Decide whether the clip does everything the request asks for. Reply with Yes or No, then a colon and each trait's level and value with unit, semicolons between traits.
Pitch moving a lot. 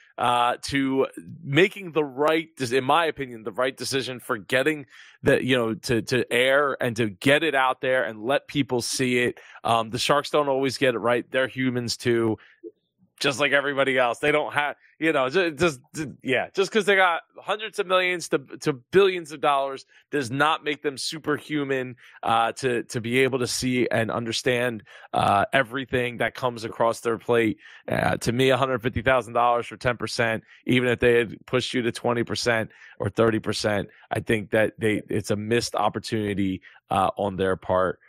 No: average, 3.7 semitones